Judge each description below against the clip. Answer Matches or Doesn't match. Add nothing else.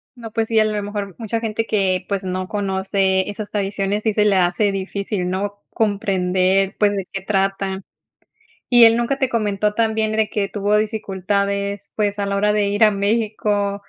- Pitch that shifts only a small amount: Matches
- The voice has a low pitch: Doesn't match